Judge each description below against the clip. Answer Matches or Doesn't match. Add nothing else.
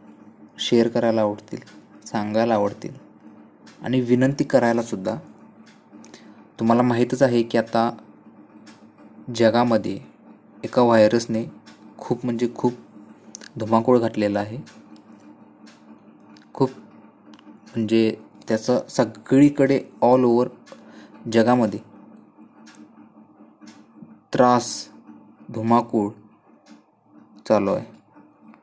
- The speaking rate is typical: Doesn't match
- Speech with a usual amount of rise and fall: Doesn't match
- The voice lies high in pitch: Doesn't match